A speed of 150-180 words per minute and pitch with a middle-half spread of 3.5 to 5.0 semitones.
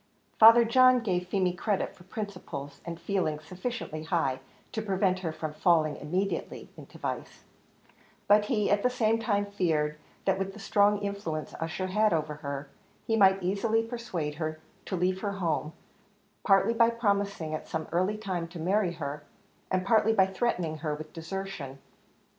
Yes: average, 165 wpm; average, 4.5 semitones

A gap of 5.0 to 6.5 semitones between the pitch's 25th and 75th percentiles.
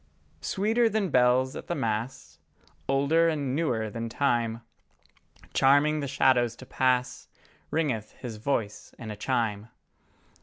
No: average, 3.8 semitones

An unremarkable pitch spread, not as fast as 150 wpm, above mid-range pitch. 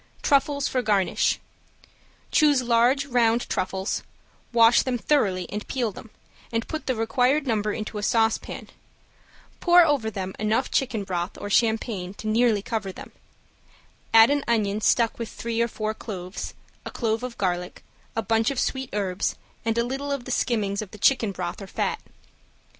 No: average, 3.4 semitones; average, 165 wpm; high, 225 Hz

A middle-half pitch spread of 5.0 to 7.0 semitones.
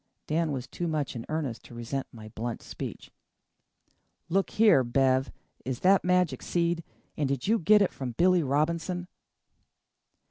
Yes: wide, 5.4 semitones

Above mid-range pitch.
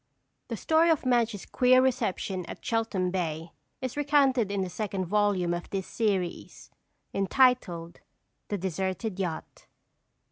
Yes: high, 200 Hz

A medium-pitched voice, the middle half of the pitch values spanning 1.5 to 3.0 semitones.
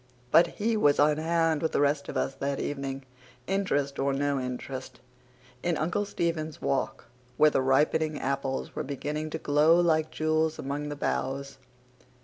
Yes: medium, 150 Hz; narrow, 2.5 semitones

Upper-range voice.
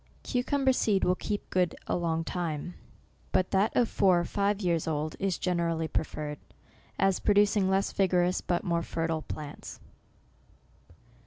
No: medium, 180 Hz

